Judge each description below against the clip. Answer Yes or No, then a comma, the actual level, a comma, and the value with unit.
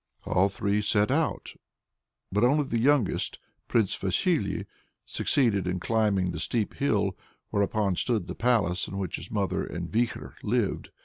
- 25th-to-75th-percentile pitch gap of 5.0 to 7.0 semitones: No, average, 3.9 semitones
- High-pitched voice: No, low, 105 Hz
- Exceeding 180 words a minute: No, average, 145 wpm